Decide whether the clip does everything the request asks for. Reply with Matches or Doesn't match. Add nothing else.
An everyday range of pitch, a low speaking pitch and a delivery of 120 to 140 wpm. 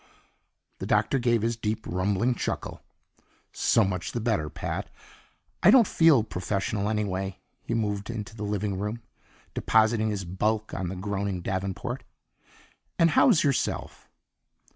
Matches